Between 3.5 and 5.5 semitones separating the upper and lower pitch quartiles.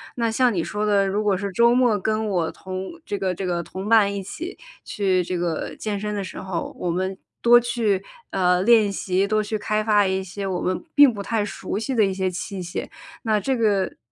No: narrow, 2.6 semitones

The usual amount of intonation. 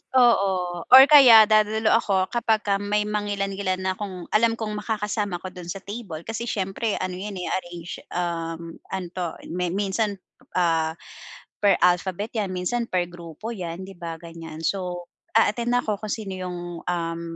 Yes: average, 3.4 semitones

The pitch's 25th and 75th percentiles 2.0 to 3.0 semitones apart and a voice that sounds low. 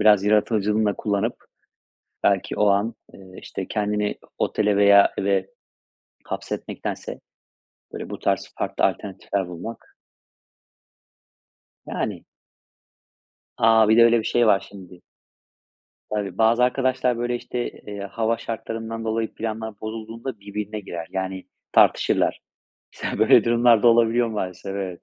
Yes: narrow, 2.4 semitones; low, 105 Hz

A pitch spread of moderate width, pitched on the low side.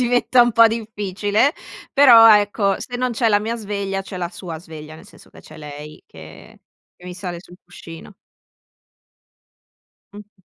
No: average, 4.5 semitones; high, 200 Hz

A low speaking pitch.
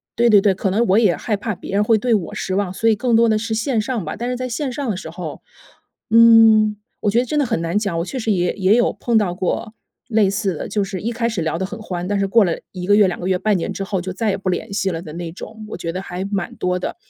No: high, 205 Hz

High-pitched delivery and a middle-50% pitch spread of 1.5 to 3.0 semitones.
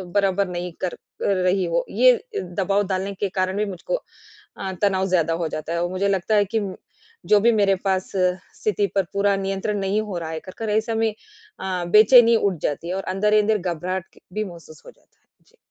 Yes: high, 195 Hz; narrow, 2.4 semitones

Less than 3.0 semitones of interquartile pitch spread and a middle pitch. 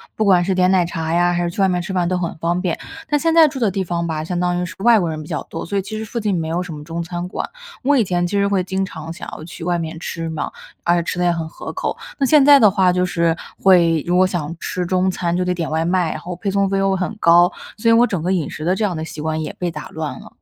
Yes: narrow, 2.4 semitones; medium, 180 Hz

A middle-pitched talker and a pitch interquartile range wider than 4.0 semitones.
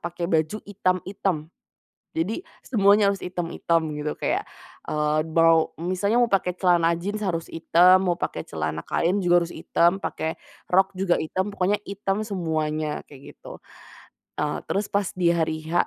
No: medium, 175 Hz; average, 3.2 semitones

